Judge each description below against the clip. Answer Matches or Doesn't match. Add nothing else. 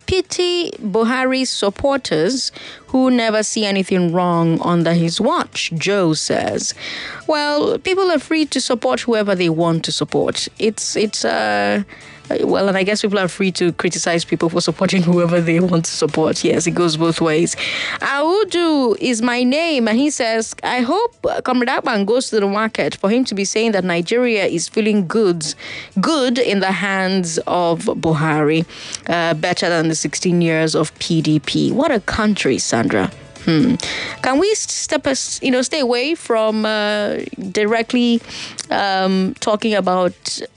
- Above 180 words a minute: Doesn't match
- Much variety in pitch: Matches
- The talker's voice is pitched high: Matches